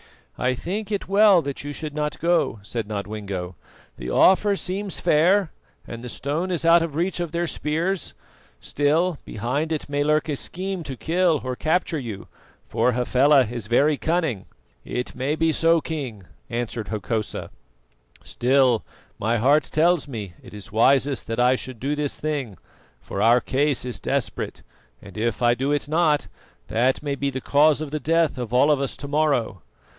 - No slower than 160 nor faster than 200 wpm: Yes, average, 175 wpm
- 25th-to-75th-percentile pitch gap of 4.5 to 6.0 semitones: Yes, average, 5.0 semitones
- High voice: No, medium, 145 Hz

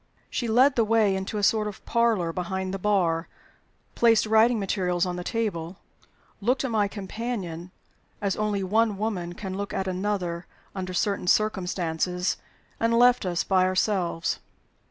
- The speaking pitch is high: Yes, high, 195 Hz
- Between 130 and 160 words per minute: Yes, average, 155 wpm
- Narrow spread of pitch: No, average, 3.4 semitones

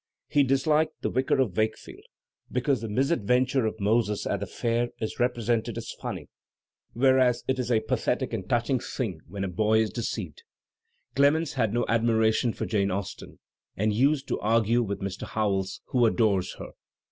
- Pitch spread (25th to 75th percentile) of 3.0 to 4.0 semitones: Yes, average, 3.3 semitones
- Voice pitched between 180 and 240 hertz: No, low, 115 Hz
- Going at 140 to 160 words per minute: No, average, 170 wpm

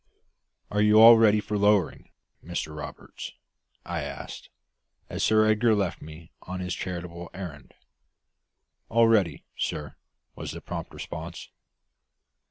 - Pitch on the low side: Yes, very low, 90 Hz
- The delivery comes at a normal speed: No, slow, 125 wpm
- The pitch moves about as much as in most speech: Yes, average, 4.2 semitones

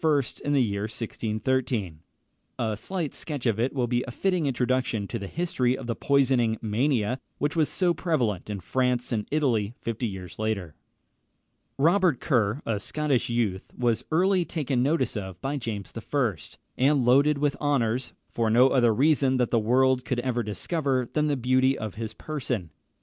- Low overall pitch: Yes, low, 125 Hz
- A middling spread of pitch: Yes, average, 4.2 semitones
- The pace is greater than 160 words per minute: Yes, average, 170 wpm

